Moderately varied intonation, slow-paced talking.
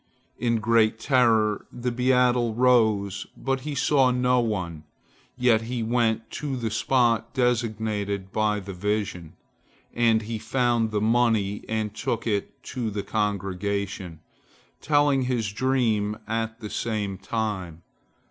Yes: average, 3.0 semitones; slow, 130 wpm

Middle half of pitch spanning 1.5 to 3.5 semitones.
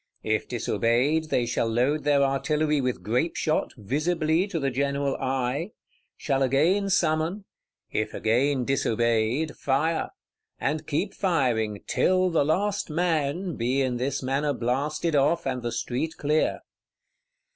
No: average, 4.0 semitones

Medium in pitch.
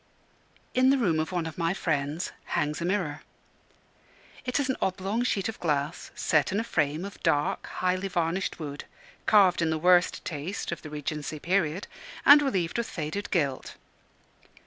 Yes: medium, 175 Hz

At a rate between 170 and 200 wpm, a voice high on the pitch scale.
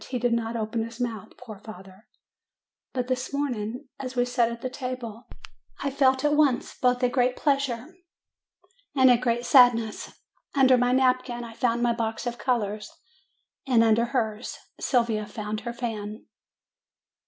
No: average, 155 wpm; high, 240 Hz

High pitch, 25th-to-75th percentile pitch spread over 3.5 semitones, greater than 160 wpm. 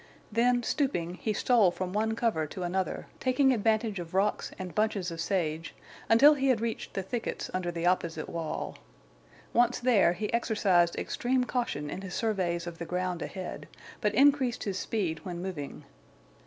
Yes: high, 195 Hz; average, 5.1 semitones; average, 170 wpm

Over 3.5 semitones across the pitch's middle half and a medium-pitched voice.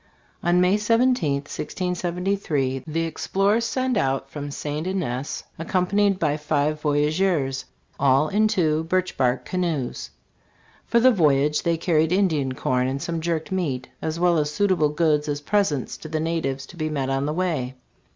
Yes: average, 4.2 semitones; medium, 160 Hz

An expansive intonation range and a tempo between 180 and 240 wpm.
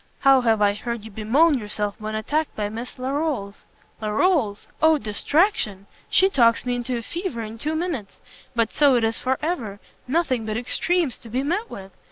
Yes: wide, 5.9 semitones; average, 185 wpm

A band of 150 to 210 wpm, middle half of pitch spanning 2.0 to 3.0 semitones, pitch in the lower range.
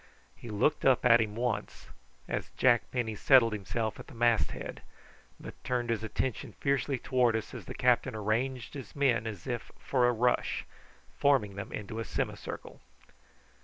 Yes: average, 165 wpm; narrow, 2.6 semitones; low, 120 Hz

